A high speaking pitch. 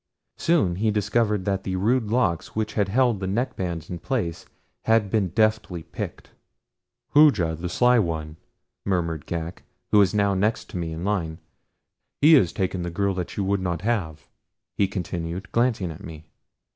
No: very low, 95 Hz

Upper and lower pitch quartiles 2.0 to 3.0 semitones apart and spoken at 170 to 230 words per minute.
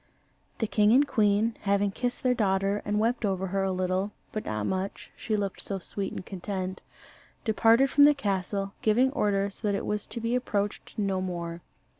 Yes: average, 2.7 semitones; average, 185 wpm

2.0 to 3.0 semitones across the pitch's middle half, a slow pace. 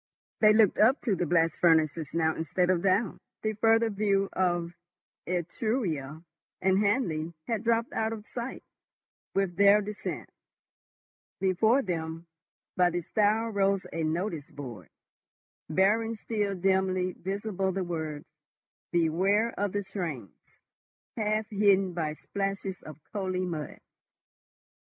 No: average, 3.8 semitones; slow, 125 wpm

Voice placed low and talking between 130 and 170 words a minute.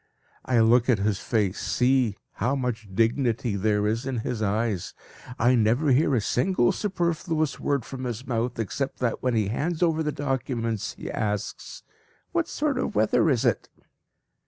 Yes: low, 120 Hz; average, 165 wpm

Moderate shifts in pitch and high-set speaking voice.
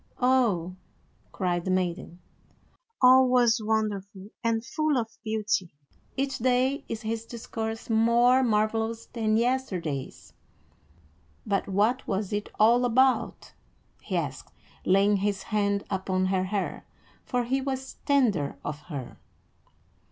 Yes: average, 4.2 semitones; high, 220 Hz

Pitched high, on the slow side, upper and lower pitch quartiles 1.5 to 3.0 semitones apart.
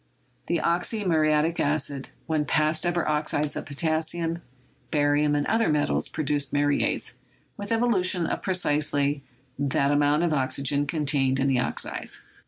No: medium, 150 Hz; slow, 130 wpm; narrow, 2.6 semitones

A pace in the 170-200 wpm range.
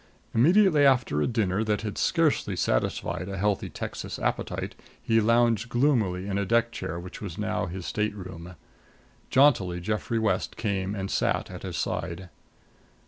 No: average, 150 wpm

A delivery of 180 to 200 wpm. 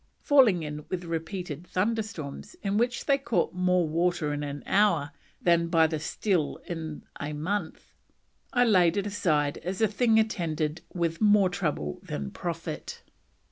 No: average, 155 wpm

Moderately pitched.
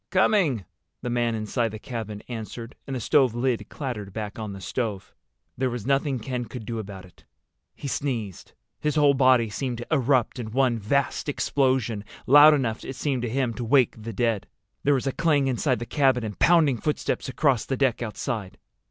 No: low, 125 Hz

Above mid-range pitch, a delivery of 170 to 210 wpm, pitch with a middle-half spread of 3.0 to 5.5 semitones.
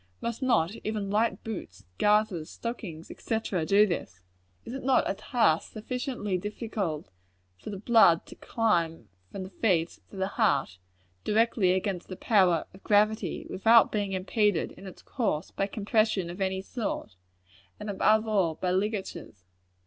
No: high, 200 Hz; average, 150 wpm; average, 3.5 semitones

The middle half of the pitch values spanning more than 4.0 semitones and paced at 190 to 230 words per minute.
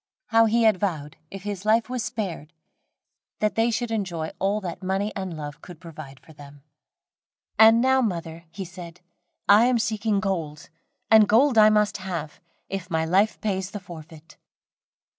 No: average, 4.7 semitones; average, 165 wpm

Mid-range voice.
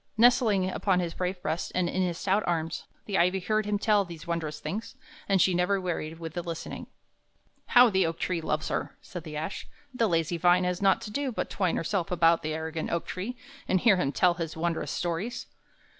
Yes: medium, 180 Hz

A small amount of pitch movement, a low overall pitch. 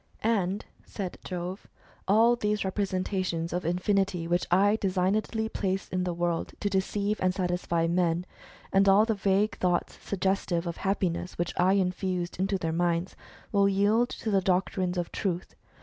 No: narrow, 2.2 semitones; medium, 185 Hz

